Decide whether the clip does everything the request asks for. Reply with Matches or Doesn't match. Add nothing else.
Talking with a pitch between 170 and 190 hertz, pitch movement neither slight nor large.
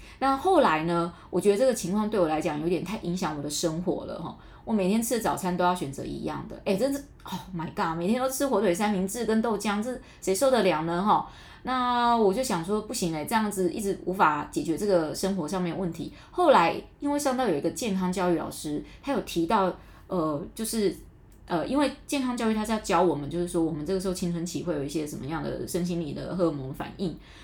Matches